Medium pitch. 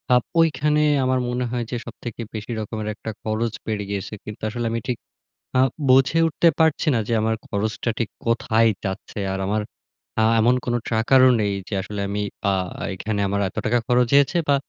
No: low, 115 Hz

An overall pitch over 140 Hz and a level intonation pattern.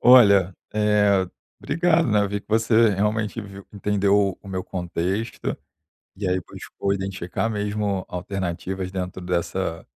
No: low, 100 Hz; narrow, 2.1 semitones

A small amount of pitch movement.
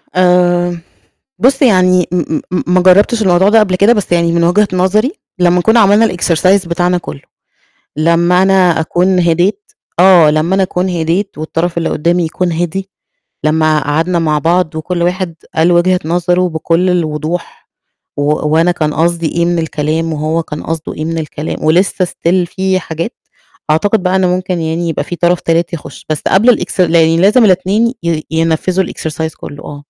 Yes: narrow, 2.3 semitones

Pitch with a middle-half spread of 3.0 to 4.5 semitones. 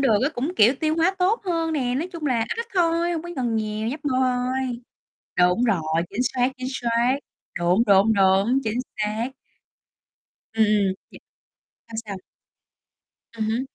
No: average, 5.0 semitones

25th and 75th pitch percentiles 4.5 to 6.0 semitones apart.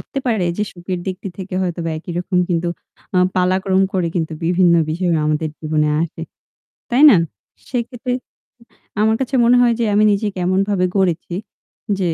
No: average, 3.3 semitones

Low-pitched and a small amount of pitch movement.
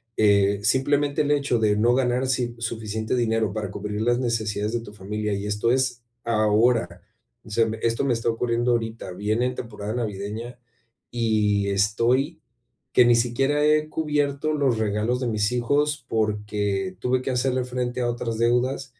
No: low, 115 Hz; average, 3.1 semitones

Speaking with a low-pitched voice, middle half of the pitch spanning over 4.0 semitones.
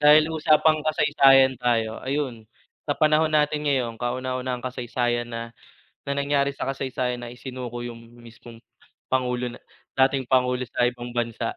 No: low, 125 Hz; narrow, 2.6 semitones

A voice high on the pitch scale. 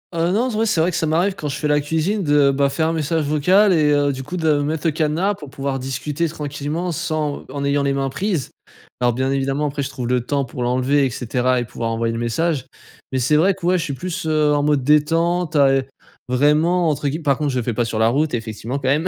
No: medium, 145 Hz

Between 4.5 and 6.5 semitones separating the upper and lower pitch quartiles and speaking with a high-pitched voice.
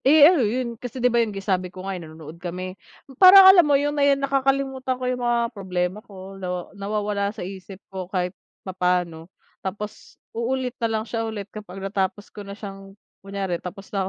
Yes: average, 5.0 semitones; high, 200 Hz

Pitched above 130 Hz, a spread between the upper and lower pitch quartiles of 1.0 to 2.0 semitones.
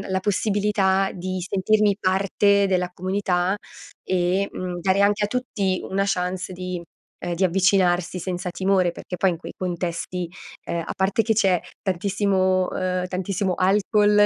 Yes: medium, 185 Hz; narrow, 1.6 semitones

